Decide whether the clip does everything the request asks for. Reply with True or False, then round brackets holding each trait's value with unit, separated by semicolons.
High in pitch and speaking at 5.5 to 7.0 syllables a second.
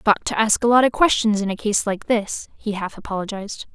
True (215 Hz; 5.6 syllables/s)